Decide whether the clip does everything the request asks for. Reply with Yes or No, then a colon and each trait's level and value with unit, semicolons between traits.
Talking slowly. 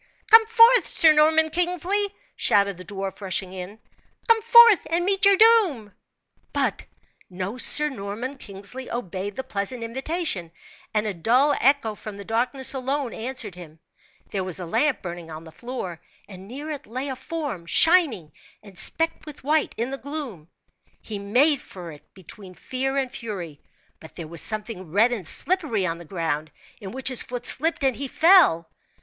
No: average, 170 wpm